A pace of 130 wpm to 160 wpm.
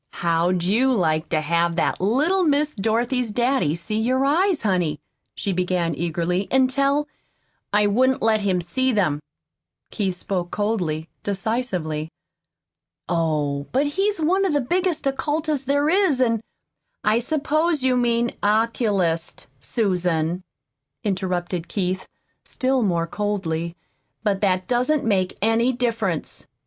Yes: slow, 135 wpm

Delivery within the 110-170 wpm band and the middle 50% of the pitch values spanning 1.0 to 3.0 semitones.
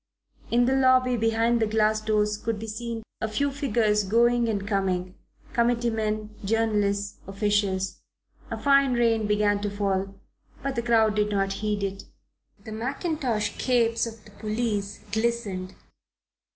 Yes: average, 145 wpm; narrow, 2.4 semitones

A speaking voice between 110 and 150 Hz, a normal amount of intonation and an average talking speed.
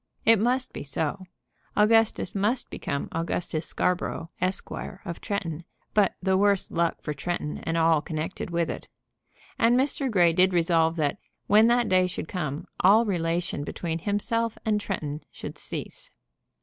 No: medium, 180 Hz; average, 4.1 semitones; average, 150 wpm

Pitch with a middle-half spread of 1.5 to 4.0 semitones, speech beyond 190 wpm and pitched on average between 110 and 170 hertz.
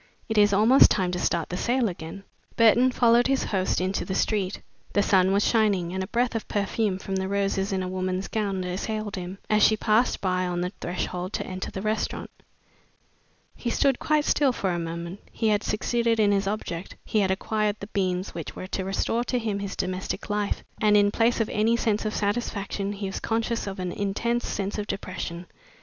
No: average, 2.9 semitones; fast, 205 wpm; high, 200 Hz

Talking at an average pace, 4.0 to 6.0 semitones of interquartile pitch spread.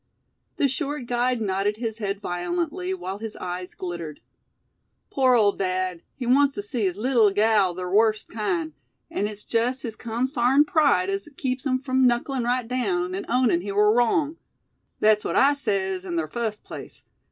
Yes: average, 175 wpm; average, 4.8 semitones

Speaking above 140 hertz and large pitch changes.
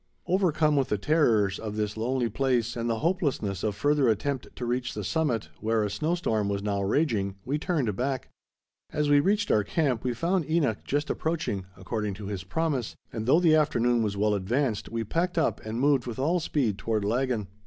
No: low, 120 Hz; wide, 6.0 semitones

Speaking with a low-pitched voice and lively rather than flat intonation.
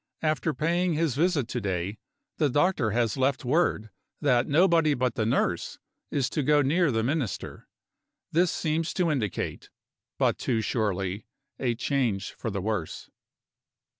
Yes: low, 130 Hz; wide, 6.0 semitones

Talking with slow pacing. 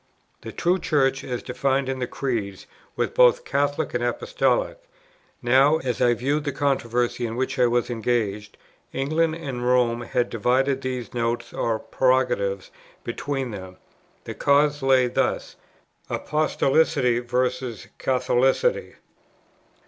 Yes: slow, 125 wpm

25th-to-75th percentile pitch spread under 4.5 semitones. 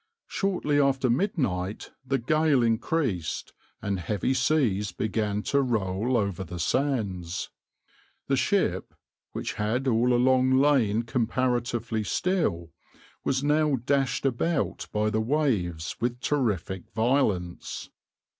No: average, 4.9 semitones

